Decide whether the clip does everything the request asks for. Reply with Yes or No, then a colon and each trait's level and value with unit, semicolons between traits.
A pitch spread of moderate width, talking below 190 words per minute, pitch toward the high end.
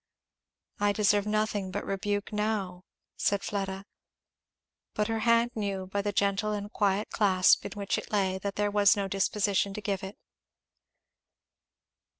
No: narrow, 1.3 semitones; average, 150 wpm; high, 205 Hz